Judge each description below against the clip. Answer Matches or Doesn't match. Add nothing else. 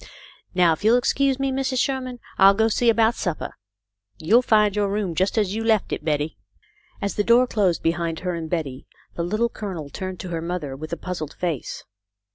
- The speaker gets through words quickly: Matches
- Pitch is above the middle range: Matches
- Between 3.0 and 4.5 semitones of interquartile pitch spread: Doesn't match